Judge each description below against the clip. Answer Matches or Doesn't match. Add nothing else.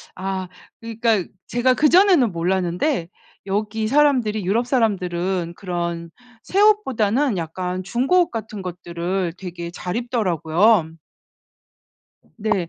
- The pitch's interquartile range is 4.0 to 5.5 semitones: Matches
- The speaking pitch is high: Matches